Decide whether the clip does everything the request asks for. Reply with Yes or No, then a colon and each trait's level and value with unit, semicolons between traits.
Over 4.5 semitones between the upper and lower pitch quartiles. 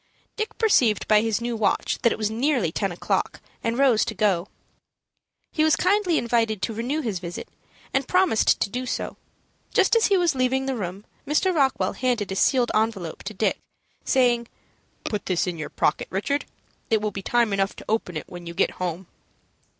Yes: average, 5.2 semitones